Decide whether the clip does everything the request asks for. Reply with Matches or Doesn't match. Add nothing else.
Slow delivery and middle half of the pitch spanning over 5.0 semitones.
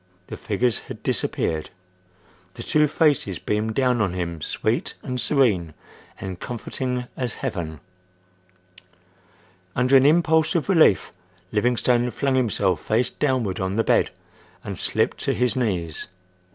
Matches